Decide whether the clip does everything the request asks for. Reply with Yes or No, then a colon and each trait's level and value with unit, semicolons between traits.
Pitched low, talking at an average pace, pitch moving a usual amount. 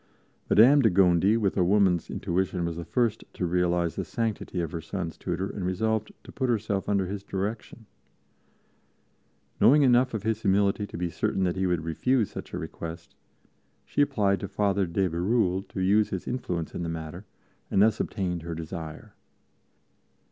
Yes: very low, 95 Hz; average, 175 wpm; average, 3.6 semitones